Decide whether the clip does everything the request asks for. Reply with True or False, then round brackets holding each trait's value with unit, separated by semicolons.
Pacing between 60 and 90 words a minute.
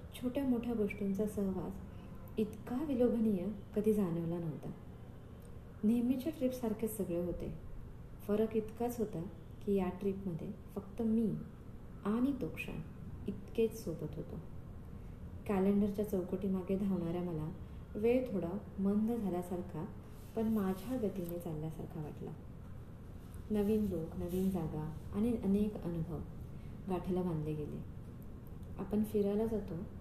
False (105 wpm)